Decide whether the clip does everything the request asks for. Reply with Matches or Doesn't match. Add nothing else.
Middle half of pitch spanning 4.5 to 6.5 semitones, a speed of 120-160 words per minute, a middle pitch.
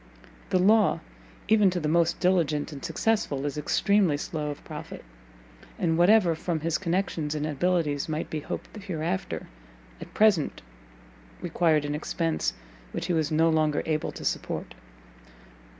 Doesn't match